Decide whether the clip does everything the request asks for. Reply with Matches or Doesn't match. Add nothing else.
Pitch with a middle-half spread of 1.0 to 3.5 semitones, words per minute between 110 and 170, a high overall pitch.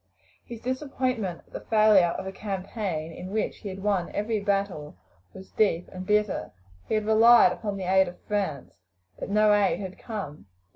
Doesn't match